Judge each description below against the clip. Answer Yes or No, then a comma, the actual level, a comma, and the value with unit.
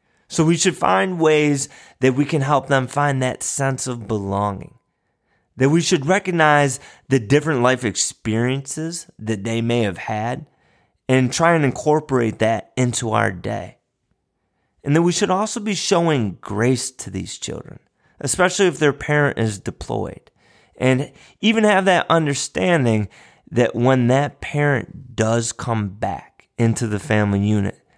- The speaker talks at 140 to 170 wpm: Yes, average, 150 wpm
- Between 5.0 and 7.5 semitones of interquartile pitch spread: Yes, wide, 5.4 semitones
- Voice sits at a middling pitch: No, low, 130 Hz